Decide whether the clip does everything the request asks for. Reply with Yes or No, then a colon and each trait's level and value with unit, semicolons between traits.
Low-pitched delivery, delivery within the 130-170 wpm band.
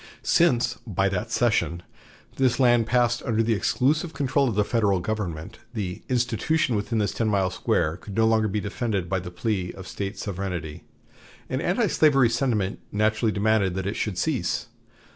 Yes: low, 110 Hz; average, 165 wpm